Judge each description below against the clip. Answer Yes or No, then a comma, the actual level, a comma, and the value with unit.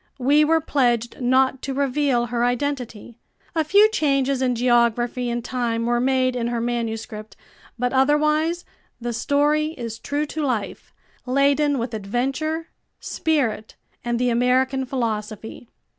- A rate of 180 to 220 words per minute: No, slow, 135 wpm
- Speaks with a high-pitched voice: Yes, very high, 250 Hz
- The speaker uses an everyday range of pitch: Yes, average, 3.2 semitones